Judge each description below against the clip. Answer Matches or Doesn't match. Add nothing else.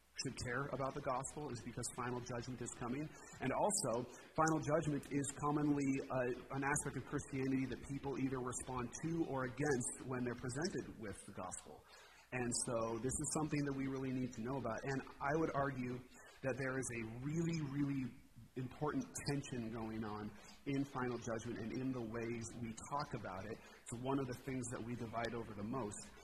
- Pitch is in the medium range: Doesn't match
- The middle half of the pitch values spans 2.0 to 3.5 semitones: Matches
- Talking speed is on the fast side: Doesn't match